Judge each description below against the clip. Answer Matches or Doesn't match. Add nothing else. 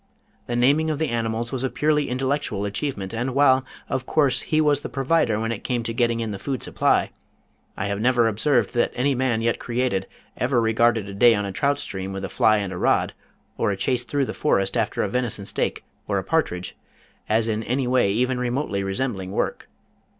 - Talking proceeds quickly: Matches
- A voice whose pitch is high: Doesn't match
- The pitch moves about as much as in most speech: Matches